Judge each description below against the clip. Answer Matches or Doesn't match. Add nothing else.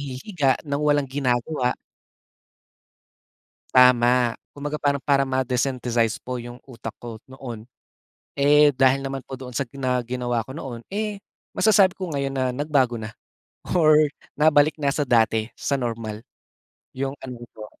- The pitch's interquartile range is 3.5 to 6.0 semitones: Doesn't match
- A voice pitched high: Doesn't match